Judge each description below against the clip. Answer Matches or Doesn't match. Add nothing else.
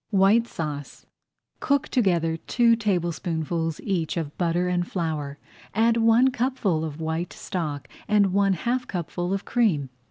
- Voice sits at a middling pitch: Matches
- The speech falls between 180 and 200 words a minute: Doesn't match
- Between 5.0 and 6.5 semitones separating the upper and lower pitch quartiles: Matches